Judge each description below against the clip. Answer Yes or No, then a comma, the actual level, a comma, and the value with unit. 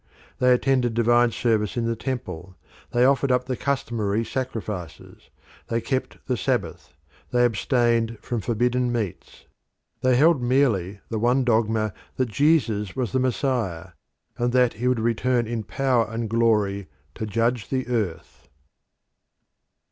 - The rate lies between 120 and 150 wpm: Yes, average, 140 wpm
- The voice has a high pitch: No, low, 120 Hz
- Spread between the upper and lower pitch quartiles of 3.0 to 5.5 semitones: No, narrow, 2.6 semitones